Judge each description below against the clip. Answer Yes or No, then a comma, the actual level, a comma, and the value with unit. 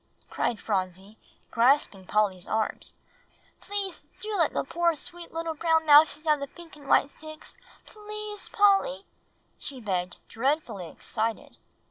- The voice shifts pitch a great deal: Yes, wide, 7.7 semitones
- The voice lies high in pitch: Yes, very high, 295 Hz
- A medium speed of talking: No, slow, 130 wpm